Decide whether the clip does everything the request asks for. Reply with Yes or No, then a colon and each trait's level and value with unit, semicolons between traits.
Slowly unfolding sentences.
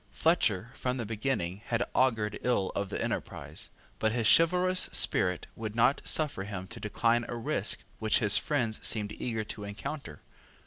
No: average, 165 wpm